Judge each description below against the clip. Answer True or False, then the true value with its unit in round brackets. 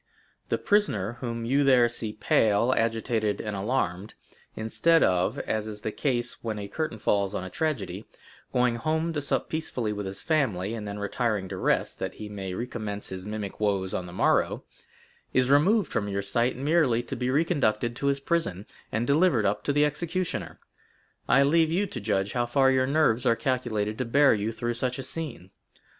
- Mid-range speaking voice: False (120 Hz)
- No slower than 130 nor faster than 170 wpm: False (180 wpm)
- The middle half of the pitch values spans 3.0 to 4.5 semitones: False (5.1 semitones)